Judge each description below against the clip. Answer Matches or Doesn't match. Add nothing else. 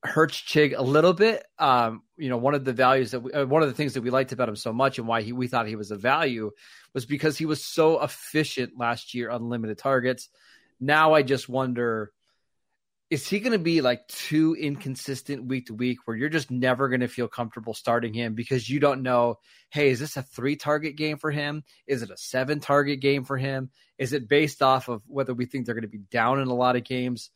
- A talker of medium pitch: Doesn't match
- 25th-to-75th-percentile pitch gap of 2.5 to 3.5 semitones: Matches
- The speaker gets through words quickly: Matches